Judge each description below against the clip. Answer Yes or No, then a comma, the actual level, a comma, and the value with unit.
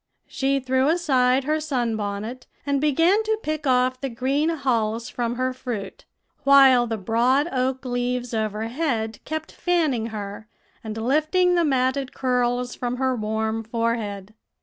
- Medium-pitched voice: No, very high, 255 Hz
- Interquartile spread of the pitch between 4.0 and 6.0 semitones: No, average, 3.4 semitones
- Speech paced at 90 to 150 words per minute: Yes, average, 145 wpm